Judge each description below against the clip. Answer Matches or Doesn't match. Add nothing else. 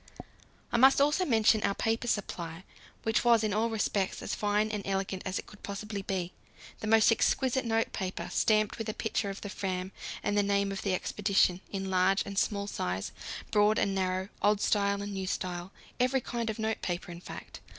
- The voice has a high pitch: Matches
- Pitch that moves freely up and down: Doesn't match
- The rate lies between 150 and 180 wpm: Doesn't match